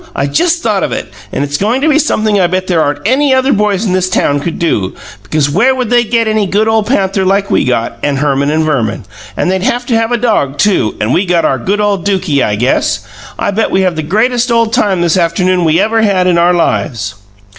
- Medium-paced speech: No, fast, 245 wpm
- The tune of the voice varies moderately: No, wide, 6.0 semitones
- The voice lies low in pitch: No, high, 190 Hz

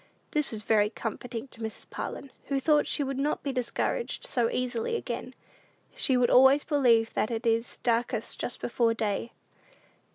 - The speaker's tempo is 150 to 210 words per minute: Yes, average, 165 wpm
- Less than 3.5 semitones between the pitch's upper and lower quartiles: Yes, average, 3.1 semitones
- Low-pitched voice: No, high, 245 Hz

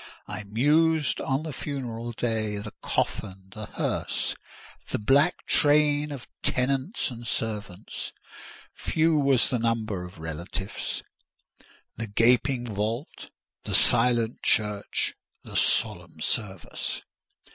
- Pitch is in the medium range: No, low, 115 Hz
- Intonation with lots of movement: No, average, 4.8 semitones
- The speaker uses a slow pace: Yes, slow, 105 wpm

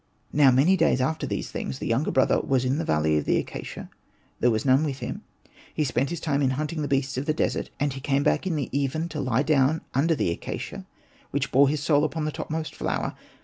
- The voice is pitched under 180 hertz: Yes, medium, 140 Hz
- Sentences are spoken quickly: Yes, fast, 235 wpm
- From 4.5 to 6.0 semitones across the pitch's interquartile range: No, average, 2.8 semitones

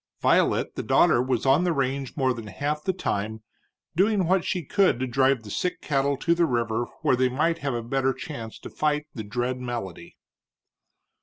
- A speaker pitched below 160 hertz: Yes, low, 135 Hz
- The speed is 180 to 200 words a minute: Yes, average, 190 wpm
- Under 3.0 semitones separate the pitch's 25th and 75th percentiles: No, average, 4.3 semitones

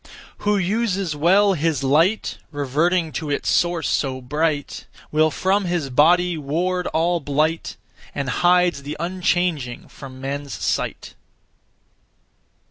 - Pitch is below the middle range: No, medium, 165 Hz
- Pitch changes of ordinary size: Yes, average, 3.8 semitones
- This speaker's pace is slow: Yes, slow, 120 wpm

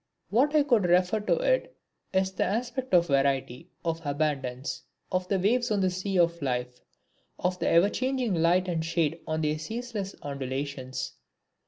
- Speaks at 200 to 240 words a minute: No, average, 160 wpm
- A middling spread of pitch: No, wide, 6.1 semitones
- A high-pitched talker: No, medium, 180 Hz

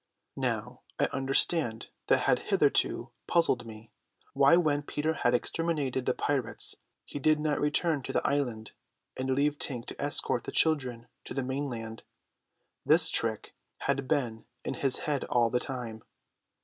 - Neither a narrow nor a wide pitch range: Yes, average, 3.4 semitones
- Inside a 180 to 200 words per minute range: No, average, 150 wpm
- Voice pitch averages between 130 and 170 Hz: Yes, low, 135 Hz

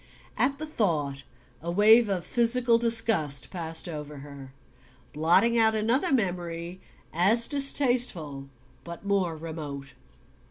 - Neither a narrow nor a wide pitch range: No, wide, 6.8 semitones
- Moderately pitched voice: Yes, medium, 180 Hz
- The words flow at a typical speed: No, slow, 115 wpm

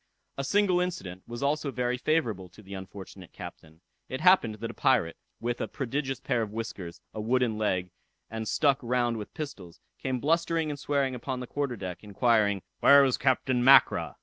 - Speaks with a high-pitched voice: No, low, 120 Hz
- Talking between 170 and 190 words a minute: Yes, average, 180 wpm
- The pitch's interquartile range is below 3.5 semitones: No, average, 5.0 semitones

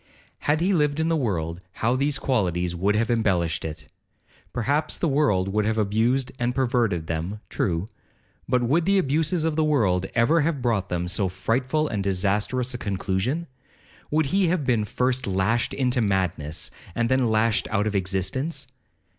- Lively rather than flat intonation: Yes, wide, 6.3 semitones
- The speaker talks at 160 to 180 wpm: Yes, average, 165 wpm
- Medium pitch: No, low, 115 Hz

